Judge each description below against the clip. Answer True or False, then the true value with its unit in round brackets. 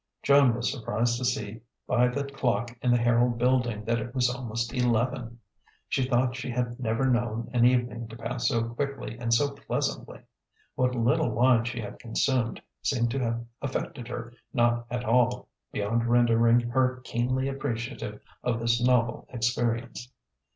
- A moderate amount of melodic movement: False (1.4 semitones)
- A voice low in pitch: True (120 Hz)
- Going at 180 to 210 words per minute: False (160 wpm)